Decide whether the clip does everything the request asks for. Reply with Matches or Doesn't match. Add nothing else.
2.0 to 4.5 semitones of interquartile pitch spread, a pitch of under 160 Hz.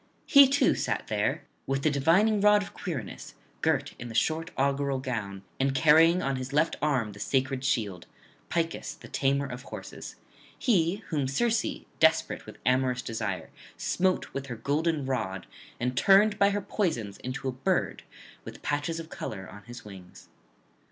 Doesn't match